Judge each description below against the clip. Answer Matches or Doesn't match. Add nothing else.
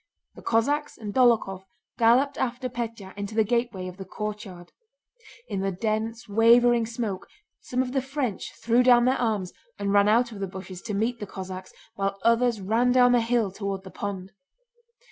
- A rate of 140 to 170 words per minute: Doesn't match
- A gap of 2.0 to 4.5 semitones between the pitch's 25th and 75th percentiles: Matches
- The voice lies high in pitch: Matches